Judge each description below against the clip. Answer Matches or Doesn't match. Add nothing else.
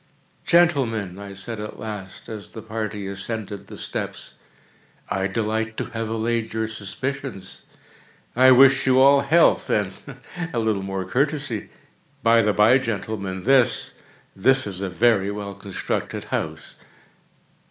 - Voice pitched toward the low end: Matches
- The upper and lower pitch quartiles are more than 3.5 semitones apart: Matches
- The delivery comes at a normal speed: Doesn't match